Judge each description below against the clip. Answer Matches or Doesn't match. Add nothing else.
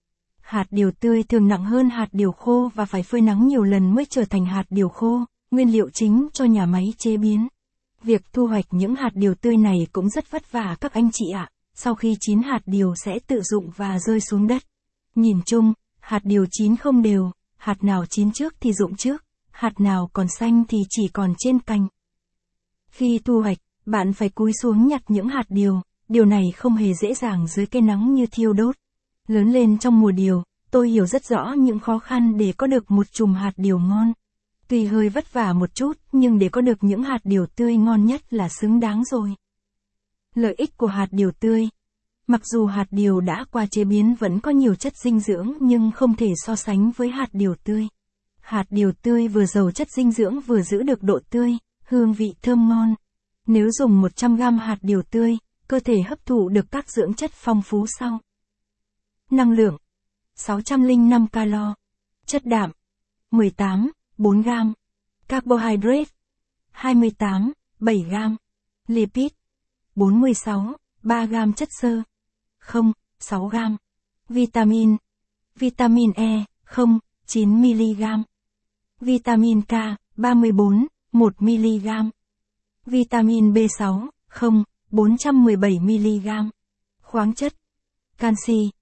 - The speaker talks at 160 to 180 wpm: Matches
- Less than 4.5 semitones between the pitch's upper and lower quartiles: Matches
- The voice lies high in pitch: Matches